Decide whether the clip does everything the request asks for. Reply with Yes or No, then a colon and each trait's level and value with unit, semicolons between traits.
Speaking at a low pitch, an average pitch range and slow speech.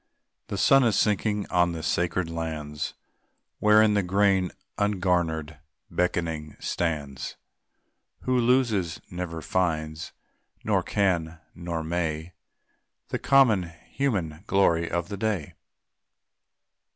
Yes: very low, 85 Hz; average, 3.9 semitones; slow, 105 wpm